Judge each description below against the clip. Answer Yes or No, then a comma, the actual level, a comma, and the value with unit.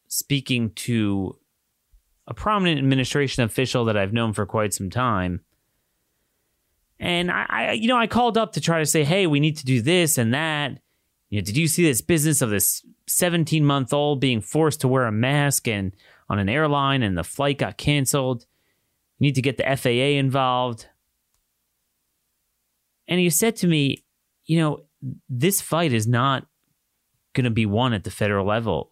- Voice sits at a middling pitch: No, low, 130 Hz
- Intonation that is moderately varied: No, wide, 6.4 semitones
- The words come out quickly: No, average, 175 wpm